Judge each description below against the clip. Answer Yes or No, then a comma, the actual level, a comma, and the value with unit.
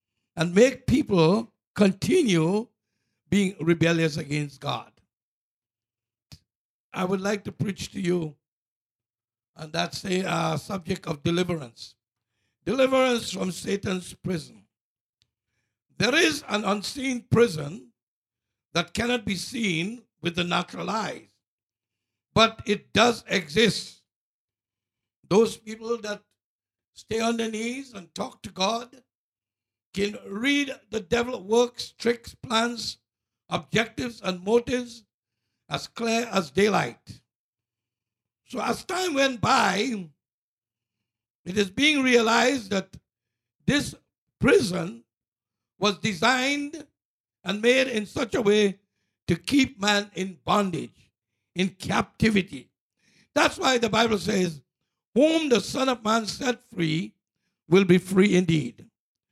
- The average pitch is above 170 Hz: Yes, medium, 185 Hz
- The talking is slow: Yes, slow, 110 wpm